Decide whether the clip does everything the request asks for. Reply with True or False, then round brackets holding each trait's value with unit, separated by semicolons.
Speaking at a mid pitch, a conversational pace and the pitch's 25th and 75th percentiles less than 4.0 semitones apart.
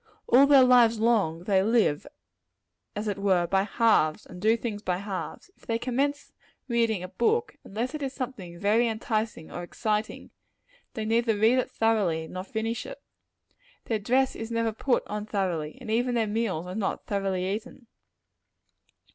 False (220 Hz; 165 wpm; 3.6 semitones)